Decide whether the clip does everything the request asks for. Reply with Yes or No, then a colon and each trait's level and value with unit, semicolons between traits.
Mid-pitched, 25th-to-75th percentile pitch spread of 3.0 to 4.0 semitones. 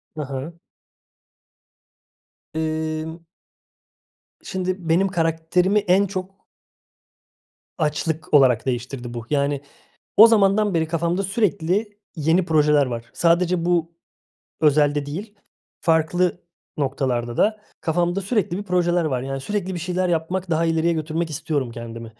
Yes: medium, 165 Hz; average, 3.7 semitones